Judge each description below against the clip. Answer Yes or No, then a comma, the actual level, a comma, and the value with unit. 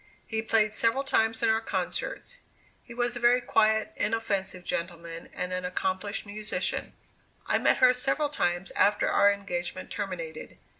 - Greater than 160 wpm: No, average, 150 wpm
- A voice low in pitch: No, high, 210 Hz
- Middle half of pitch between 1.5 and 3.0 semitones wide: No, average, 3.9 semitones